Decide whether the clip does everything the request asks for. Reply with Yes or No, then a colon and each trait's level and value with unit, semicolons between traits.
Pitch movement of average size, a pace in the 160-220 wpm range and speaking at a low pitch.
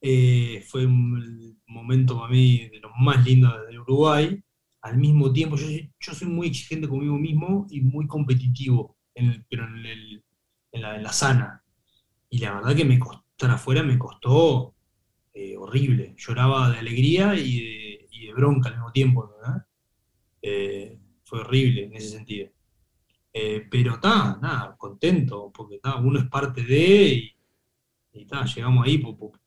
Yes: average, 3.3 semitones; average, 165 wpm; low, 125 Hz